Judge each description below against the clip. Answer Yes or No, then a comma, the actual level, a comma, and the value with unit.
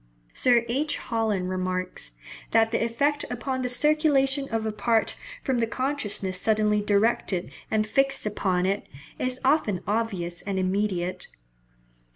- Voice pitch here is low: No, high, 220 Hz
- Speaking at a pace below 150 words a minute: Yes, slow, 135 wpm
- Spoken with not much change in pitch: No, average, 4.6 semitones